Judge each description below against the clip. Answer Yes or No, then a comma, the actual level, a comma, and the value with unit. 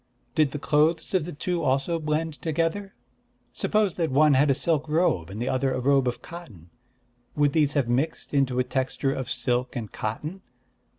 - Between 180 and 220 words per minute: Yes, average, 185 wpm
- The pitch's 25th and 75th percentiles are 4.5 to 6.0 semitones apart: No, average, 3.9 semitones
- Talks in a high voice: No, medium, 145 Hz